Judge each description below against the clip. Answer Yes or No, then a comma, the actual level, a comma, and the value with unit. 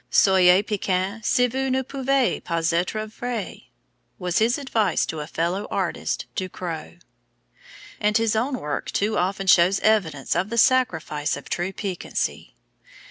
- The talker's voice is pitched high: Yes, high, 200 Hz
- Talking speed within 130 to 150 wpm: Yes, average, 145 wpm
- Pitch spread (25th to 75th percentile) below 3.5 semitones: No, average, 4.5 semitones